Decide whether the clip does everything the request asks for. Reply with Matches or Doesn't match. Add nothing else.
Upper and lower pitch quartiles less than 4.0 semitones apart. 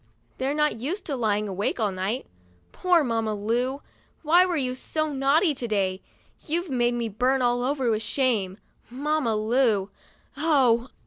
Doesn't match